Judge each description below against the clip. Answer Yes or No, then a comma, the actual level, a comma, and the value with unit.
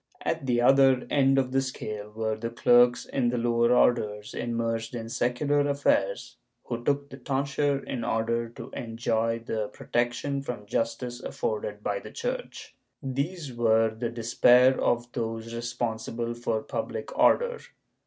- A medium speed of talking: Yes, average, 150 wpm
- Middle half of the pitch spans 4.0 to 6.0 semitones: No, average, 2.8 semitones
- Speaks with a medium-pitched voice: No, low, 120 Hz